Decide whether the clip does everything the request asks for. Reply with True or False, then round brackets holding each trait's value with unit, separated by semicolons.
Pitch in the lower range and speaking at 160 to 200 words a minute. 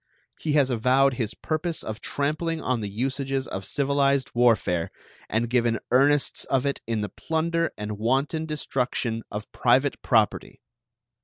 False (130 Hz; 145 wpm)